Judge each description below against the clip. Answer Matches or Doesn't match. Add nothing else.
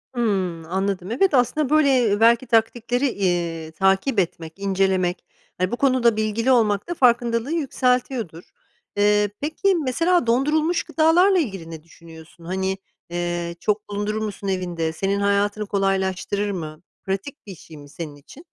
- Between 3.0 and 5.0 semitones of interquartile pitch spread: Doesn't match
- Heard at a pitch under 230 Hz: Matches